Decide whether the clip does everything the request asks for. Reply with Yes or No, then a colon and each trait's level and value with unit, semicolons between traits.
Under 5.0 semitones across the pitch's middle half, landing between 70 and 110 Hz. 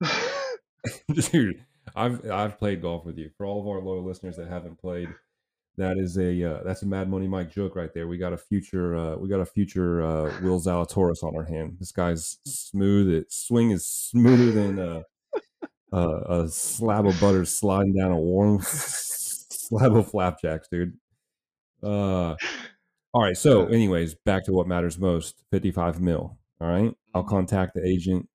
Yes: average, 2.8 semitones; very low, 95 Hz